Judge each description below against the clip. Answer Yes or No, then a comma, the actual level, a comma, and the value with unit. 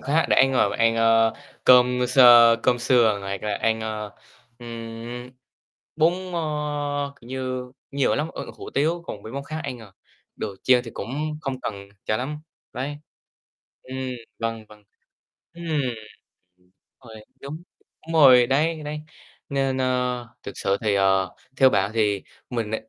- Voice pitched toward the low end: Yes, low, 125 Hz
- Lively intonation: No, average, 3.9 semitones